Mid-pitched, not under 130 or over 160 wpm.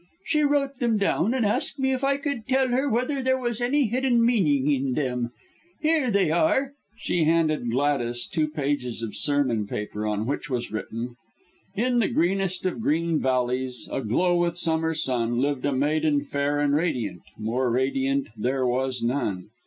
No: medium, 150 Hz; average, 175 wpm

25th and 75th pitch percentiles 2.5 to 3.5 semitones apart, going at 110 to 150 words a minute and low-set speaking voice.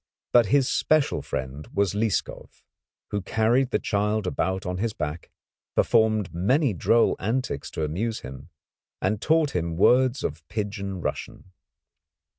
No: average, 4.7 semitones; slow, 135 wpm; low, 105 Hz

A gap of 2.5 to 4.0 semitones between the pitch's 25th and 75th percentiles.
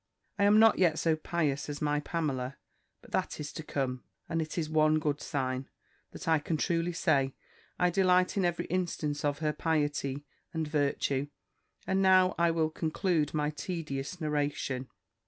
Yes: average, 2.8 semitones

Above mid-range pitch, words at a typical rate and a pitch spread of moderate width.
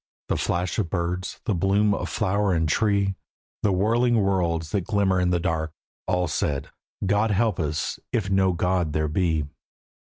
No: very low, 95 Hz; average, 165 wpm; average, 3.3 semitones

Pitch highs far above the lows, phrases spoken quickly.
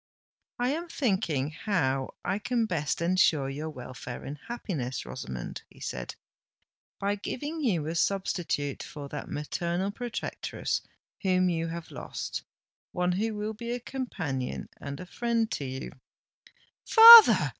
No: wide, 7.6 semitones; slow, 135 wpm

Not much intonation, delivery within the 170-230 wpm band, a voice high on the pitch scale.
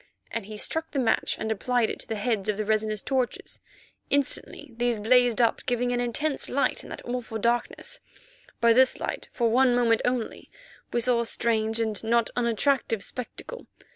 Yes: narrow, 2.1 semitones; average, 180 wpm; high, 235 Hz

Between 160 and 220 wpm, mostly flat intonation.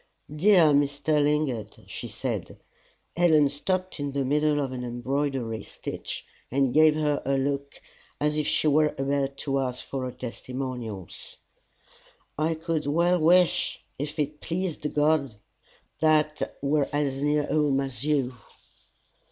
No: average, 140 wpm; narrow, 2.1 semitones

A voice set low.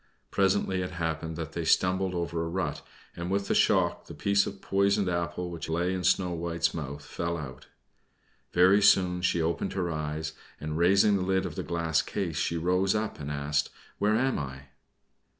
Yes: very low, 85 Hz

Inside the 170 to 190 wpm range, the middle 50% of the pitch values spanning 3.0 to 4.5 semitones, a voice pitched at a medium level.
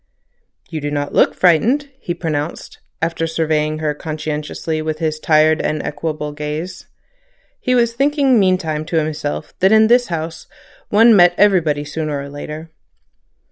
No: average, 145 wpm; average, 3.4 semitones; medium, 160 Hz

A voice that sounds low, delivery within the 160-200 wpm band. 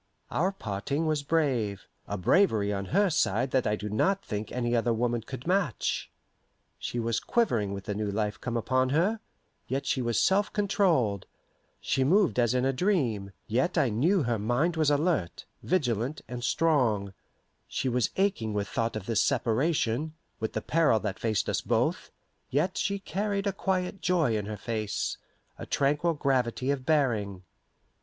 Yes: low, 130 Hz; average, 170 wpm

